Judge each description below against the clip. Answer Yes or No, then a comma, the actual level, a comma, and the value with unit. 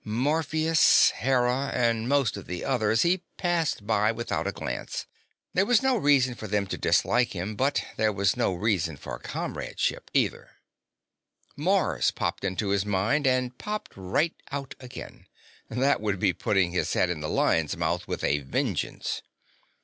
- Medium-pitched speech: No, low, 115 Hz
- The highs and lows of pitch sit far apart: Yes, wide, 6.2 semitones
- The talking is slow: No, average, 160 wpm